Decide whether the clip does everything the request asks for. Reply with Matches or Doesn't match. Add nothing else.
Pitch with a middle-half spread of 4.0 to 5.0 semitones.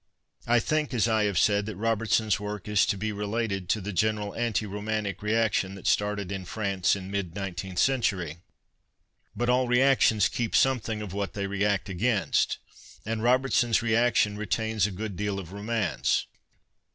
Doesn't match